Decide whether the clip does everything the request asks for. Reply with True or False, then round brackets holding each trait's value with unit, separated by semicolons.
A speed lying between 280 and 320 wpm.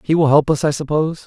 True (285 wpm)